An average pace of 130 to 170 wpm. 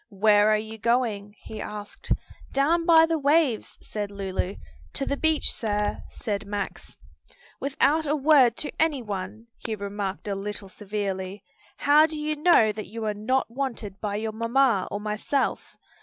Yes: average, 160 wpm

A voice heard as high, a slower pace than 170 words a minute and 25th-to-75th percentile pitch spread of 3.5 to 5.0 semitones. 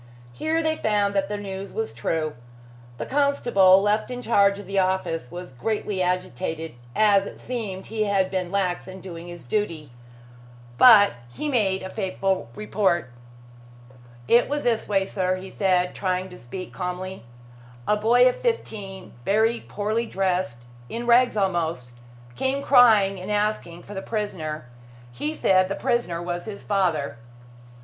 No: high, 195 Hz; average, 155 wpm; average, 3.1 semitones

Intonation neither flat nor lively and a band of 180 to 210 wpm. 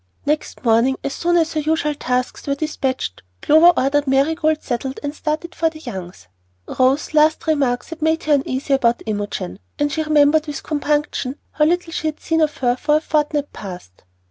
Yes: average, 3.2 semitones; average, 185 wpm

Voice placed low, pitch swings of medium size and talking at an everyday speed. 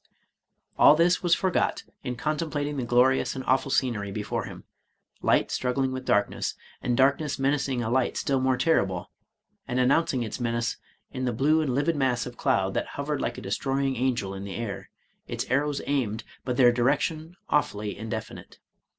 Yes: low, 130 Hz; average, 3.3 semitones; average, 175 wpm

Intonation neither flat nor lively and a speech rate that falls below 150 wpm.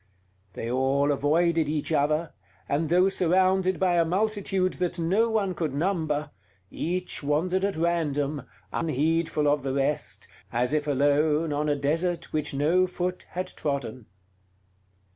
Yes: average, 3.7 semitones; average, 140 wpm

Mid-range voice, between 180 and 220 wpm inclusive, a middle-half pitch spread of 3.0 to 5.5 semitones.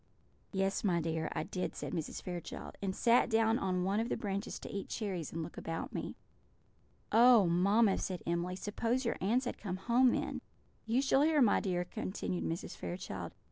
No: high, 195 Hz; average, 185 wpm; average, 4.6 semitones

